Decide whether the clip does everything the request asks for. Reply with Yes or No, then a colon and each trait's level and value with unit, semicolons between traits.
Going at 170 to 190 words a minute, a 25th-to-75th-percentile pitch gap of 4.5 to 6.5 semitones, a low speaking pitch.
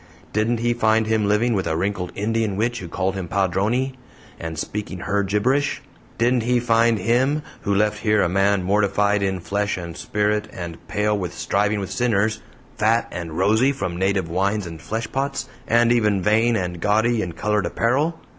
No: average, 175 wpm; average, 3.3 semitones; low, 105 Hz